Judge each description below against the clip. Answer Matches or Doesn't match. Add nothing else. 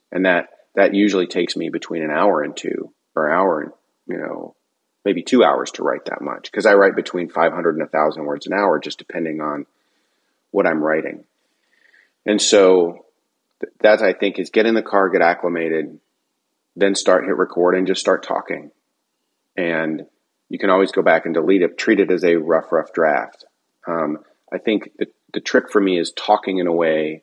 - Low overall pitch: Matches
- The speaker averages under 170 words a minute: Doesn't match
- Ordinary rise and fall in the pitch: Matches